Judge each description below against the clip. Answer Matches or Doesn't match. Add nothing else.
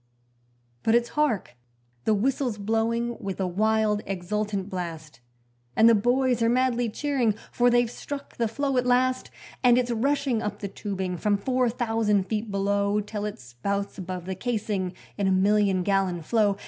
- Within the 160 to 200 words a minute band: Matches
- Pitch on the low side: Doesn't match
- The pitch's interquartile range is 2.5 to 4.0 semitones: Matches